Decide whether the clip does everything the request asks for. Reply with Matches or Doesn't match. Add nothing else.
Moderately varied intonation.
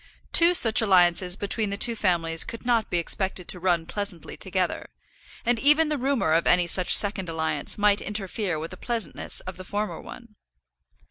Matches